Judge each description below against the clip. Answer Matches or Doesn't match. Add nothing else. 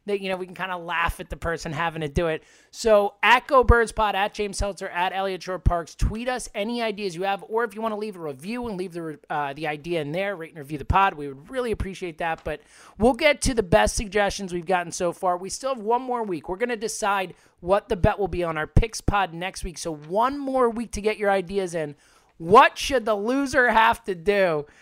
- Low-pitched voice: Doesn't match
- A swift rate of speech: Matches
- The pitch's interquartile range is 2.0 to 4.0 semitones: Doesn't match